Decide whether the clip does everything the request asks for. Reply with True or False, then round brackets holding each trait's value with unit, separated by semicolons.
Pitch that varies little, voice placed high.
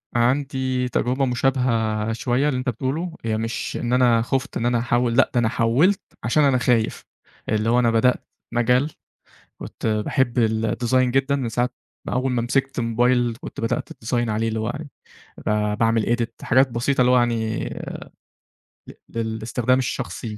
False (2.2 semitones; 120 Hz)